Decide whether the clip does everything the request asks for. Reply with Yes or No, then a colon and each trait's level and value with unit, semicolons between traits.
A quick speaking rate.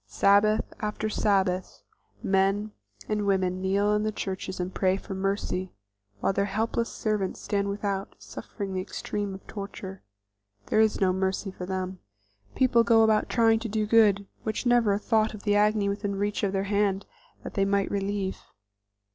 No: average, 170 wpm